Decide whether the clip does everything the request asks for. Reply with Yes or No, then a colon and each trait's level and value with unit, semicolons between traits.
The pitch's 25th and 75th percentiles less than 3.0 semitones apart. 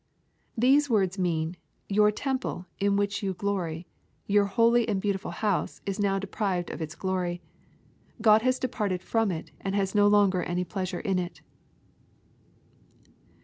Yes: narrow, 2.6 semitones